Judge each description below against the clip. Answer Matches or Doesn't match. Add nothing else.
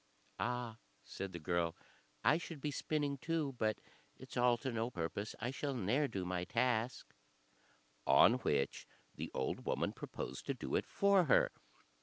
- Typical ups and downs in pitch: Doesn't match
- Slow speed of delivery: Doesn't match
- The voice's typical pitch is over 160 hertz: Doesn't match